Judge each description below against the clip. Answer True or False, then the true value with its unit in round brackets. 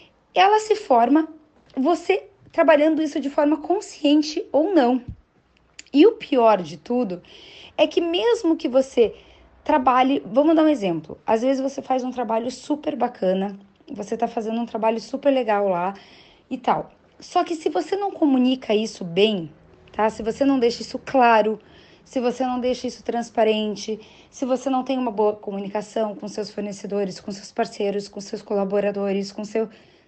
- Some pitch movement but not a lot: False (6.2 semitones)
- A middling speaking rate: True (165 wpm)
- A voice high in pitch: True (245 Hz)